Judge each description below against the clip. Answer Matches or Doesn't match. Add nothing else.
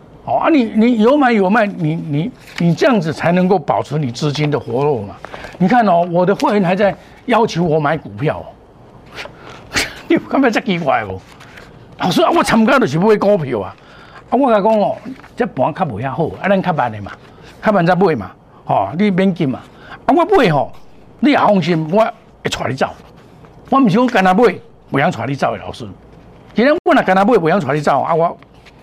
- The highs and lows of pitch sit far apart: Matches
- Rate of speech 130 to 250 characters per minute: Doesn't match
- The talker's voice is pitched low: Doesn't match